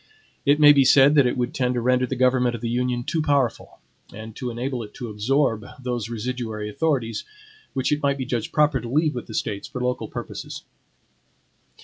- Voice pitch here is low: Yes, low, 125 Hz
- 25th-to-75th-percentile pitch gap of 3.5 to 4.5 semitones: No, average, 2.7 semitones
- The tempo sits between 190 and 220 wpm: Yes, fast, 205 wpm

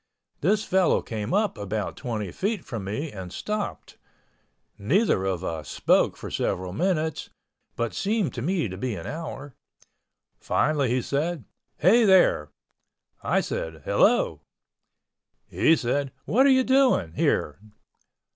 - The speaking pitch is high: No, medium, 140 Hz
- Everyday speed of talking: No, slow, 125 wpm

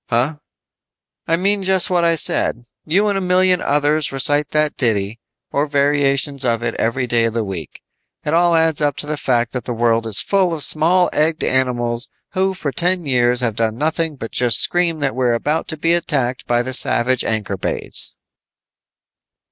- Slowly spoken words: No, average, 185 wpm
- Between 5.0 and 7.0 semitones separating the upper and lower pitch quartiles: Yes, wide, 5.5 semitones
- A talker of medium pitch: Yes, medium, 145 Hz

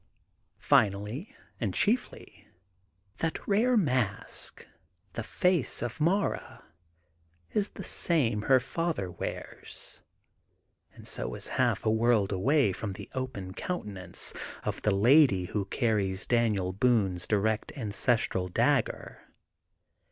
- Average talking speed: No, slow, 115 wpm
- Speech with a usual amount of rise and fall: No, wide, 6.8 semitones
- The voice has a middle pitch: No, low, 110 Hz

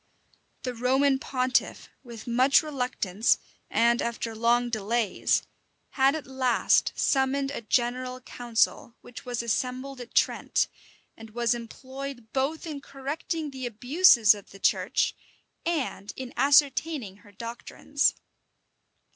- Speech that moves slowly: Yes, slow, 120 wpm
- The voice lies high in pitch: Yes, very high, 250 Hz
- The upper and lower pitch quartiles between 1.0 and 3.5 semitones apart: Yes, average, 2.8 semitones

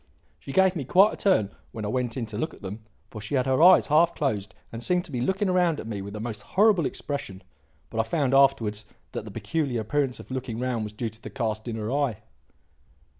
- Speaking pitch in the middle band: No, low, 125 Hz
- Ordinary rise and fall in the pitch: No, wide, 5.9 semitones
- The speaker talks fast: Yes, fast, 240 wpm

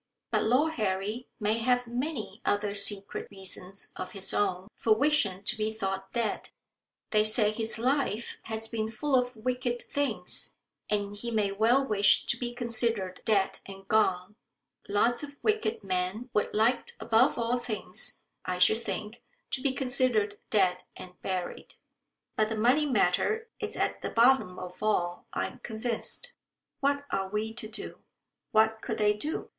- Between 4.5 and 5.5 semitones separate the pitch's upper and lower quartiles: No, average, 3.6 semitones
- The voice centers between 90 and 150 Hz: No, high, 220 Hz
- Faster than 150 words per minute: Yes, average, 160 wpm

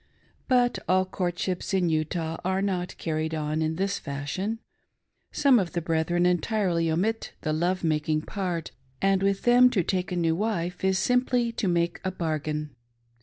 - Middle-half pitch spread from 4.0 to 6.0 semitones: No, average, 3.4 semitones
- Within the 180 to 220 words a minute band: No, average, 165 wpm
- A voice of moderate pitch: Yes, medium, 180 Hz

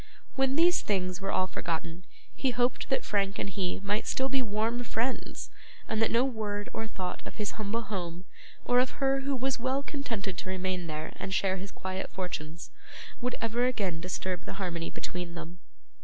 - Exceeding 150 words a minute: Yes, average, 185 wpm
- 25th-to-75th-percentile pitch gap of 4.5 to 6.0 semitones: Yes, average, 5.1 semitones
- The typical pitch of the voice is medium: No, high, 205 Hz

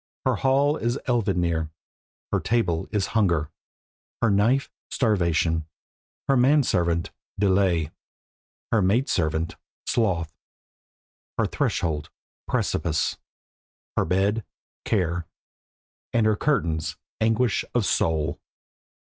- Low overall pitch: Yes, very low, 95 Hz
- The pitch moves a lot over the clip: Yes, wide, 5.8 semitones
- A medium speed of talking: No, slow, 100 wpm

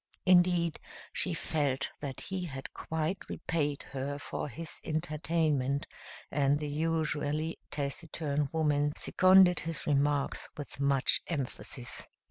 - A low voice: No, medium, 150 Hz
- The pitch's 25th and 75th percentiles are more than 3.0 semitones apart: No, narrow, 2.6 semitones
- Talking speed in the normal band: No, slow, 110 wpm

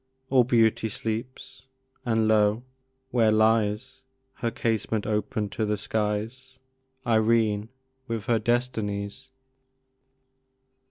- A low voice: Yes, low, 110 Hz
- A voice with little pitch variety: Yes, narrow, 2.0 semitones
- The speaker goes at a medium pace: No, slow, 95 wpm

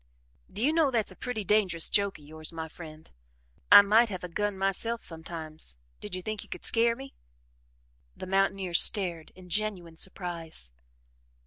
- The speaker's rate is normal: Yes, average, 170 wpm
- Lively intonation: No, average, 4.5 semitones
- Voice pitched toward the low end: No, high, 190 Hz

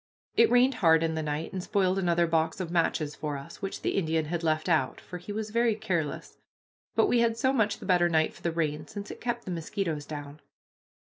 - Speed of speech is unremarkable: No, fast, 230 wpm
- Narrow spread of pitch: No, average, 4.5 semitones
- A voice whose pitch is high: No, medium, 170 Hz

